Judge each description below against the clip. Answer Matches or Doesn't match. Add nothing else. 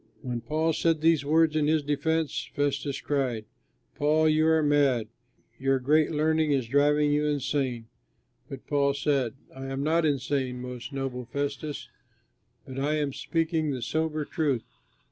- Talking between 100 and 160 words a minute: Matches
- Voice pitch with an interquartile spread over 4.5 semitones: Doesn't match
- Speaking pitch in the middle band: Matches